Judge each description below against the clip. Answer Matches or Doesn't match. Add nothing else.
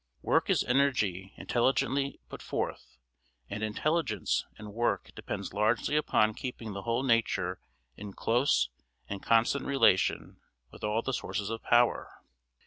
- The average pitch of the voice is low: Matches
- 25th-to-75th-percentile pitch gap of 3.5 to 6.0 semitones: Matches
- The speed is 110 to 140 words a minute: Matches